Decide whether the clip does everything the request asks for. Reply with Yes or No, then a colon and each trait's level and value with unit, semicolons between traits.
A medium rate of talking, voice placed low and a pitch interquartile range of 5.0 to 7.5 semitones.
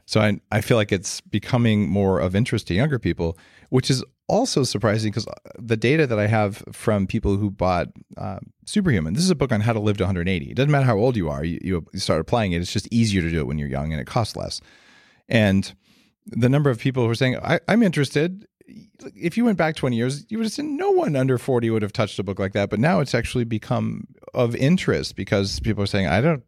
No: fast, 245 wpm; low, 110 Hz; wide, 5.4 semitones